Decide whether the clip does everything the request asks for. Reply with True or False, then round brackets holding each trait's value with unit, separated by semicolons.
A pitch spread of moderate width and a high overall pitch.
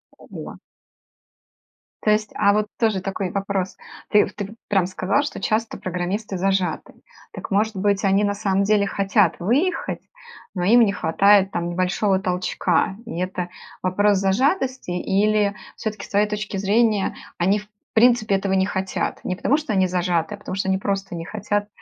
False (2.0 semitones; 200 Hz)